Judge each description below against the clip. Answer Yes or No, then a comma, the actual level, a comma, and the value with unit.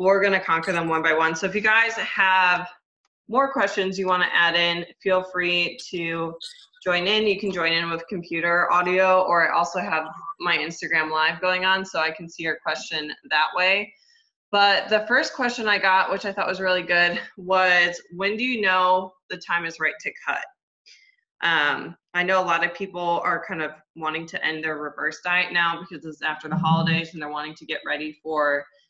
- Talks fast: Yes, fast, 210 wpm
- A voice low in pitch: No, medium, 175 Hz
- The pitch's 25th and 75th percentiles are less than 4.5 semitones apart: Yes, narrow, 2.6 semitones